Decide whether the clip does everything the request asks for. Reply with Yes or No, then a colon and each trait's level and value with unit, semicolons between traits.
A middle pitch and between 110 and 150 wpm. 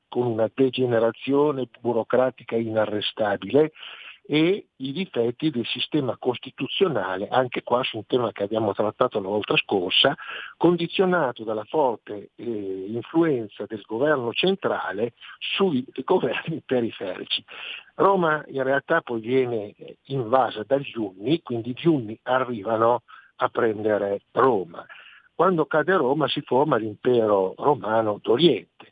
No: low, 125 Hz; slow, 115 wpm